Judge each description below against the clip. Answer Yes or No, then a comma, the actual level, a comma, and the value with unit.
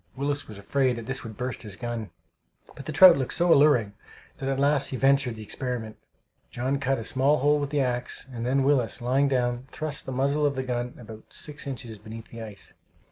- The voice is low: Yes, low, 130 Hz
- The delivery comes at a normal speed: No, fast, 215 wpm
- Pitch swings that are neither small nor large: Yes, average, 3.0 semitones